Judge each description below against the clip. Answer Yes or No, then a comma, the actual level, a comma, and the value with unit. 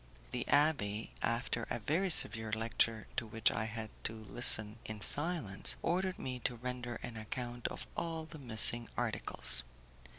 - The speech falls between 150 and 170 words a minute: Yes, average, 155 wpm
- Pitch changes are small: No, average, 4.0 semitones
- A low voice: Yes, low, 120 Hz